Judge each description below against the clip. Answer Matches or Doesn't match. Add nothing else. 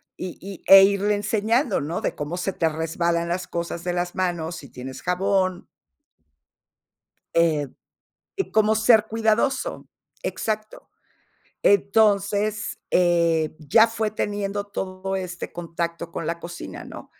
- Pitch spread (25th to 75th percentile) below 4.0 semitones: Matches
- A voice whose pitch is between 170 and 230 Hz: Matches